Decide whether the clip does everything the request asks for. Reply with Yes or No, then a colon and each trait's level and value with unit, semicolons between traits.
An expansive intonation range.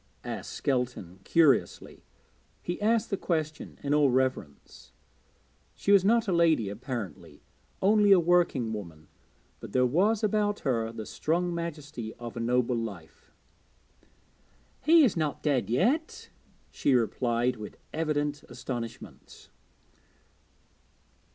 Yes: wide, 7.1 semitones